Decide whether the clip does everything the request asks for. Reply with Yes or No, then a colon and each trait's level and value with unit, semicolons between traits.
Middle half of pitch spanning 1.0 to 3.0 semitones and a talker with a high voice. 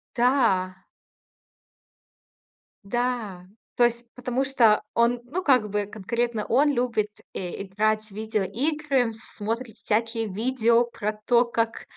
Yes: average, 2.7 semitones; high, 230 Hz